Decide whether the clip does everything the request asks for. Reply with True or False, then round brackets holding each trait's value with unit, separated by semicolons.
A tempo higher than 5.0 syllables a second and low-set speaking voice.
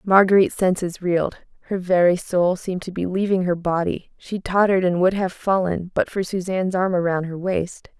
False (5.2 syllables/s; 185 Hz)